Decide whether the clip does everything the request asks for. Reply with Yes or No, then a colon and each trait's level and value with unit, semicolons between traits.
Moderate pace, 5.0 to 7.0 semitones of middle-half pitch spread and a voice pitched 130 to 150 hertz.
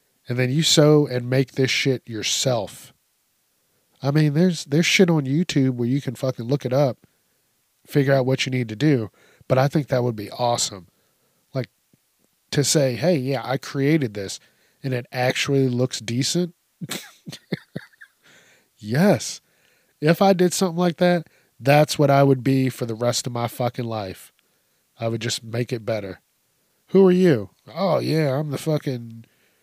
No: average, 170 wpm; average, 3.7 semitones; low, 135 Hz